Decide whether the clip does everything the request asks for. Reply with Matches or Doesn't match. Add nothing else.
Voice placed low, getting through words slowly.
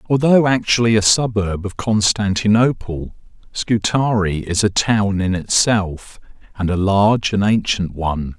Matches